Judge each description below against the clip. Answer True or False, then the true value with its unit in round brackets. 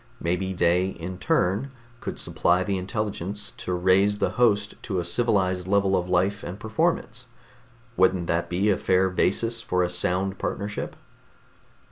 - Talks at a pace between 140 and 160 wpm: True (150 wpm)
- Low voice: True (95 Hz)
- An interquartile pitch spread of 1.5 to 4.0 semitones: True (2.4 semitones)